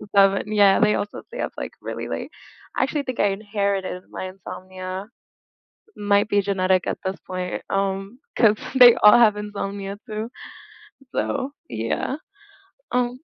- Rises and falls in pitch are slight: Yes, narrow, 1.9 semitones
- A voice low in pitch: No, high, 200 Hz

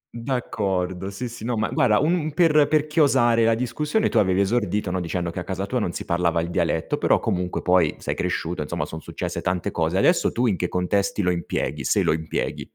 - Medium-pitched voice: No, low, 100 Hz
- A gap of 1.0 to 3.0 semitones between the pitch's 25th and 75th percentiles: No, wide, 5.5 semitones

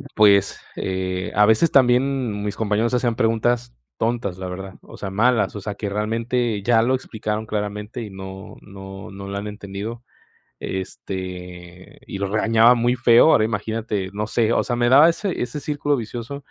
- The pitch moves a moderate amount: Yes, average, 3.5 semitones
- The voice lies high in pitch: No, low, 110 Hz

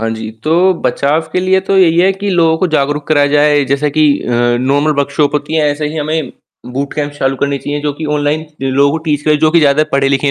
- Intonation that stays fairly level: Yes, narrow, 2.0 semitones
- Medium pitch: Yes, medium, 145 Hz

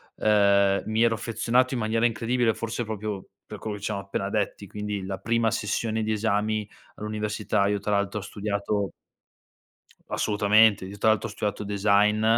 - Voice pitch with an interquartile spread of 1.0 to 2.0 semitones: Yes, narrow, 1.4 semitones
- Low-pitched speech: Yes, low, 105 Hz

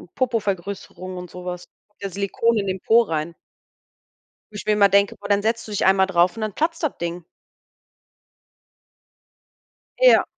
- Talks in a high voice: Yes, high, 200 Hz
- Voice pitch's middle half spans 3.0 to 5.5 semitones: Yes, average, 3.3 semitones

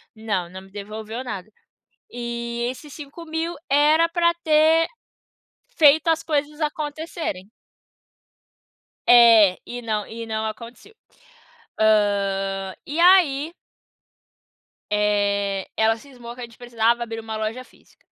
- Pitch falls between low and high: No, high, 235 Hz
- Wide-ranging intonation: Yes, wide, 5.9 semitones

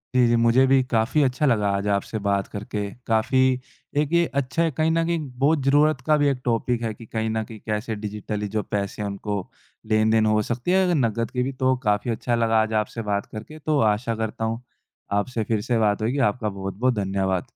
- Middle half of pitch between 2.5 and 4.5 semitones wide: Yes, average, 3.6 semitones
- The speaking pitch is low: Yes, low, 115 Hz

